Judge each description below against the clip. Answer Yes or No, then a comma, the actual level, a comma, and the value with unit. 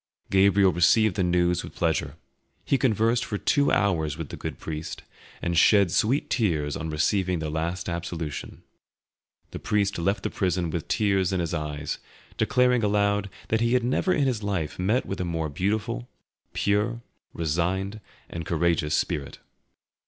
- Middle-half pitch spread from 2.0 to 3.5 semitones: No, average, 4.2 semitones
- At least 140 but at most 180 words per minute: Yes, average, 160 wpm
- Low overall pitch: Yes, very low, 95 Hz